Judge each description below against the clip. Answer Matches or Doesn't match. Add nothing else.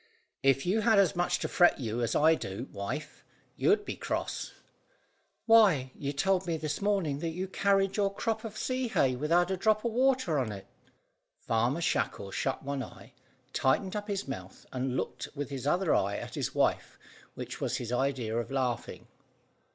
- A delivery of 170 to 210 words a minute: Matches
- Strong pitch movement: Matches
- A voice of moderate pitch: Matches